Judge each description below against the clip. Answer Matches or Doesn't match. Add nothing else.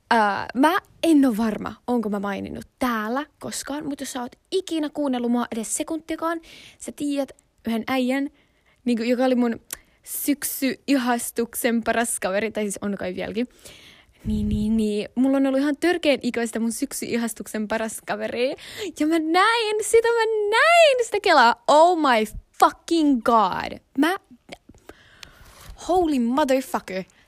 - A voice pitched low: Doesn't match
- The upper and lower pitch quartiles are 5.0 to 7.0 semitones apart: Matches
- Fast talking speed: Doesn't match